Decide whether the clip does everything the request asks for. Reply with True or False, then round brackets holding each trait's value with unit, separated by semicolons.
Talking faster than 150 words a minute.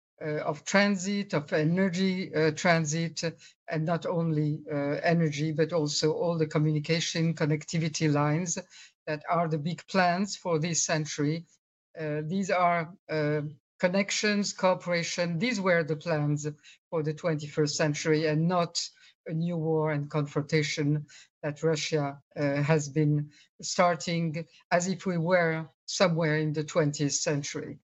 False (135 wpm)